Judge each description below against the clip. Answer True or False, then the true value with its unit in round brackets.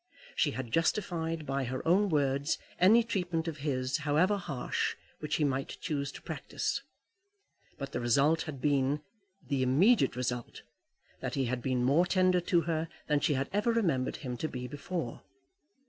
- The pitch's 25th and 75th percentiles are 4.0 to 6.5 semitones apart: True (4.5 semitones)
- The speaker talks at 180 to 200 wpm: False (165 wpm)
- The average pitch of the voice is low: False (150 Hz)